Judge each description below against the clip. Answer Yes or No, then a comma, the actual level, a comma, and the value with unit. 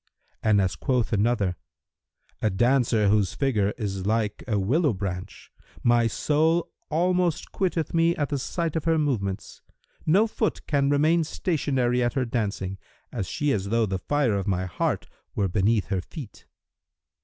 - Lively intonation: Yes, wide, 6.8 semitones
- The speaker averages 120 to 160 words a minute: Yes, average, 155 wpm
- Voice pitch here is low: Yes, low, 120 Hz